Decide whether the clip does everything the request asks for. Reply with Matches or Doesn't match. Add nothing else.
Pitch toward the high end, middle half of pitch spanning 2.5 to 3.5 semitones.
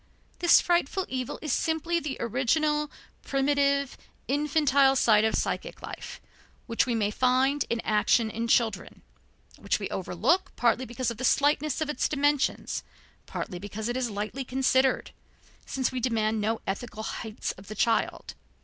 Doesn't match